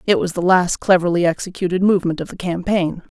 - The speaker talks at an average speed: Yes, average, 190 wpm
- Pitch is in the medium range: Yes, medium, 180 Hz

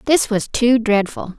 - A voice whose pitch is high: Yes, high, 230 Hz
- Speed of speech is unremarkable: Yes, average, 175 wpm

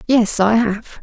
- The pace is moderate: Yes, average, 175 wpm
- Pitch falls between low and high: No, high, 220 Hz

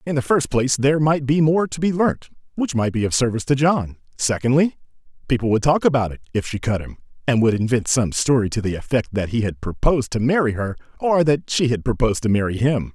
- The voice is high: No, low, 125 Hz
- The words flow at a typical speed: No, fast, 235 wpm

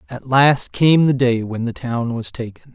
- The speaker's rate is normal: No, fast, 220 wpm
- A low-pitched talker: Yes, low, 125 Hz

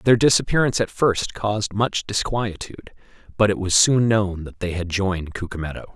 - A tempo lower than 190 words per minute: Yes, average, 170 wpm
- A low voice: Yes, low, 100 Hz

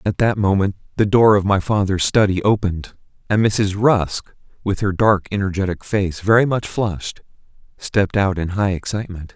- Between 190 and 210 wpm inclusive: No, average, 165 wpm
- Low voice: Yes, low, 100 Hz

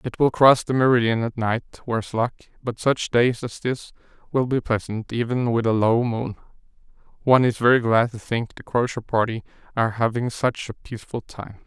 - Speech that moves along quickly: No, average, 190 wpm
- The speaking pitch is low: Yes, low, 120 Hz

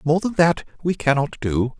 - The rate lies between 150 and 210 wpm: Yes, average, 200 wpm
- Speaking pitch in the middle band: Yes, medium, 155 Hz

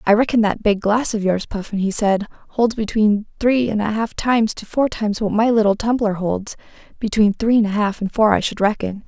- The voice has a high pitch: Yes, high, 215 Hz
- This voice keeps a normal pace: No, fast, 230 wpm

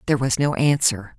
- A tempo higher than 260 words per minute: No, average, 200 wpm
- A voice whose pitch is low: Yes, low, 130 Hz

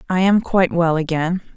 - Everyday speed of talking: Yes, average, 190 wpm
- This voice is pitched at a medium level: Yes, medium, 175 Hz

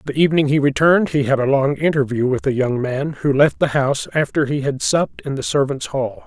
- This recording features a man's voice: Yes, male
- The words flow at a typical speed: No, fast, 240 wpm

